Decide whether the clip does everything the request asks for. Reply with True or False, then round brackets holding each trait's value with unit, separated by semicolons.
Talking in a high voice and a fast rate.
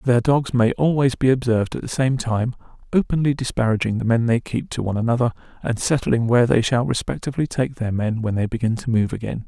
False (120 Hz; 215 wpm)